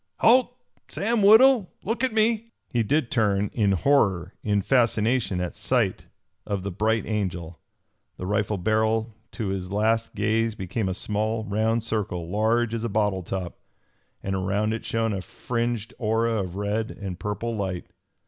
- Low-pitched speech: Yes, low, 110 Hz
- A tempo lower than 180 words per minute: Yes, average, 160 wpm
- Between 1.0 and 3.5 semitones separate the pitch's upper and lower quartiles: Yes, average, 2.8 semitones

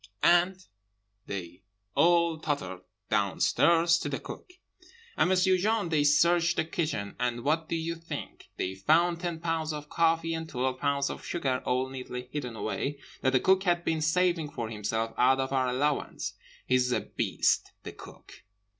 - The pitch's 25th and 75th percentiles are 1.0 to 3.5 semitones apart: No, average, 4.9 semitones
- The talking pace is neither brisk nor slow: Yes, average, 165 wpm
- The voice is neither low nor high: Yes, medium, 155 Hz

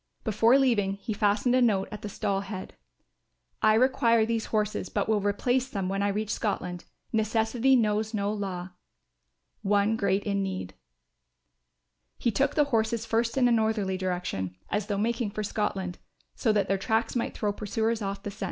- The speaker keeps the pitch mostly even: Yes, narrow, 2.3 semitones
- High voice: Yes, high, 210 Hz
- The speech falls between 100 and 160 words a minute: No, average, 175 wpm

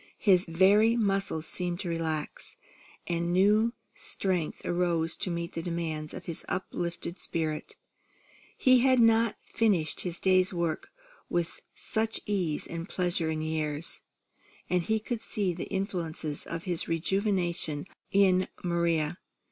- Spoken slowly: Yes, slow, 130 wpm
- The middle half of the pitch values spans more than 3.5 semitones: No, average, 3.0 semitones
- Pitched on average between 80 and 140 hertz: No, medium, 175 Hz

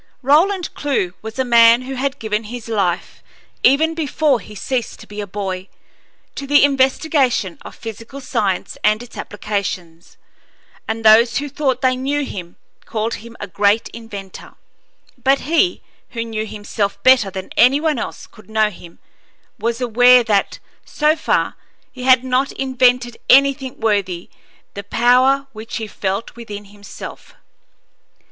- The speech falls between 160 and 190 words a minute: No, average, 150 wpm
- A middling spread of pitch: Yes, average, 4.3 semitones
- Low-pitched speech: No, high, 235 Hz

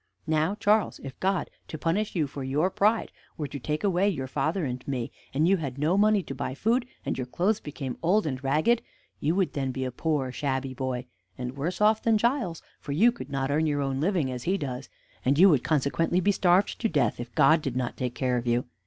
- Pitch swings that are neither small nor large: No, wide, 6.2 semitones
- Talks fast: Yes, fast, 230 wpm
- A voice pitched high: No, medium, 150 Hz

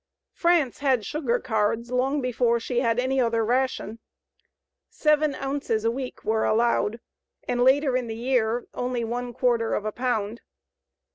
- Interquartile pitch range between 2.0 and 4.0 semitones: Yes, narrow, 2.4 semitones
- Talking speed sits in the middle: Yes, average, 150 wpm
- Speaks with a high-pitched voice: Yes, high, 245 Hz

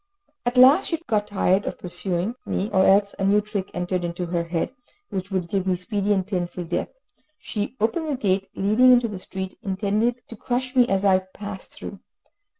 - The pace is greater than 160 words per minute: Yes, average, 195 wpm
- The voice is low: No, high, 200 Hz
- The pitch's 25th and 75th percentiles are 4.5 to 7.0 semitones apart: No, average, 3.1 semitones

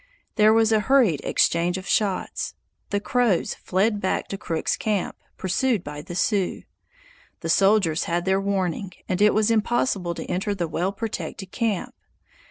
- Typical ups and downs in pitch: Yes, average, 3.3 semitones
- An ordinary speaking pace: Yes, average, 160 wpm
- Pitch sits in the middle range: No, high, 195 Hz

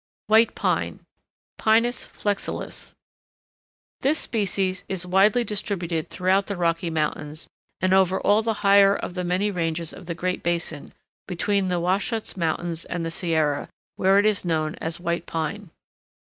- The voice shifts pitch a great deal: No, average, 3.2 semitones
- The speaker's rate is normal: Yes, average, 145 wpm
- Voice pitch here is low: No, medium, 185 Hz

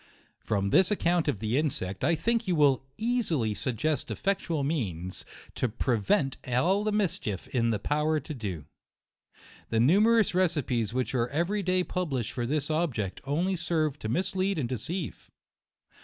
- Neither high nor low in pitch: Yes, medium, 150 Hz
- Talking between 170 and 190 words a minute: No, average, 155 wpm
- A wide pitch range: Yes, wide, 7.4 semitones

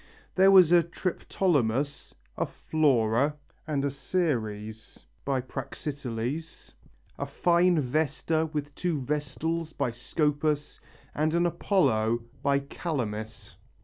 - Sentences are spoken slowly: Yes, slow, 105 wpm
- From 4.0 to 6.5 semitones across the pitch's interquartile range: Yes, average, 4.7 semitones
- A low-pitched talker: No, medium, 145 Hz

